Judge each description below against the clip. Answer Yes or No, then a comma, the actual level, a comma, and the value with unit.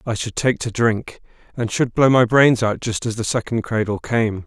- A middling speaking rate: No, fast, 230 wpm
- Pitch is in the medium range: No, low, 115 Hz